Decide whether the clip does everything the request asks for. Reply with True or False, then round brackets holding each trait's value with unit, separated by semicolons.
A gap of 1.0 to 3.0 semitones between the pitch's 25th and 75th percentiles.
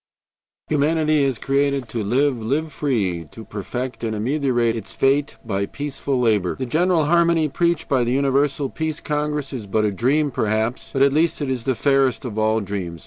False (4.8 semitones)